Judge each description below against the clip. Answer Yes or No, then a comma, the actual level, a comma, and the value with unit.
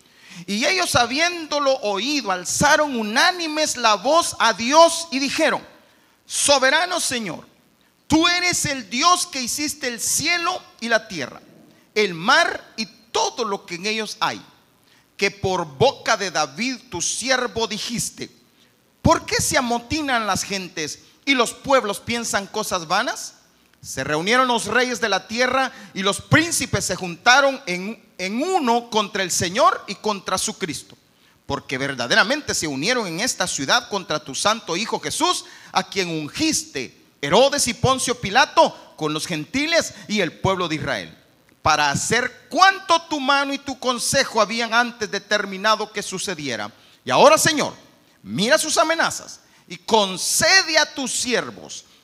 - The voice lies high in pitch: Yes, high, 230 Hz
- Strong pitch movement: Yes, wide, 6.4 semitones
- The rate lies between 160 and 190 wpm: No, average, 145 wpm